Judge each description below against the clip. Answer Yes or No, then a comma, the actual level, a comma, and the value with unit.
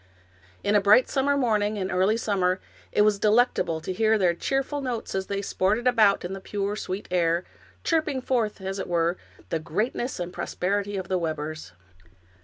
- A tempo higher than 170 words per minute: Yes, average, 180 wpm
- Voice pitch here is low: No, high, 200 Hz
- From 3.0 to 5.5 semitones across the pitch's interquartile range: Yes, average, 3.7 semitones